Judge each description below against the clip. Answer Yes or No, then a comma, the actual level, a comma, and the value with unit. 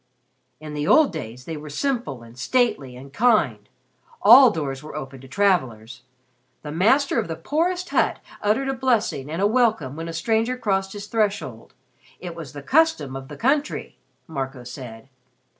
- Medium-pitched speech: Yes, medium, 165 Hz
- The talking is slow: No, average, 170 wpm